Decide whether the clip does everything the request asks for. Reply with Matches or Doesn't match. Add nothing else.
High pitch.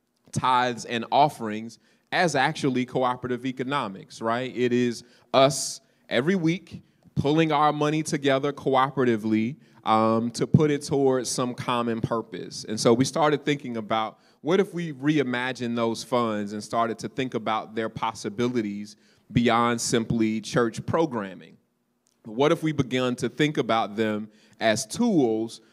Doesn't match